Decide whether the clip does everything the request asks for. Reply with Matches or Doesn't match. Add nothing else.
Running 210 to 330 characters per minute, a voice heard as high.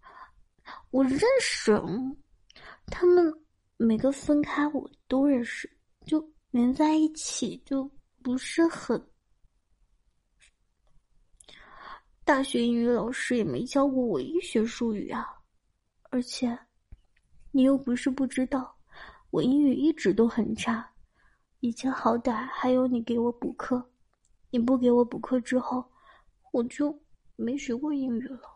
Doesn't match